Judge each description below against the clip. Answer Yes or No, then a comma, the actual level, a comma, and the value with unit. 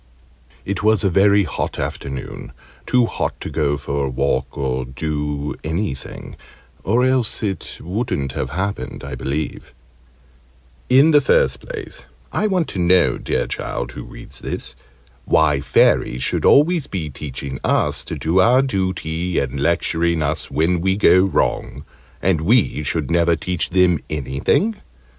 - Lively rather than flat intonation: Yes, wide, 6.1 semitones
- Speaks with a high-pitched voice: No, very low, 85 Hz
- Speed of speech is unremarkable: Yes, average, 150 wpm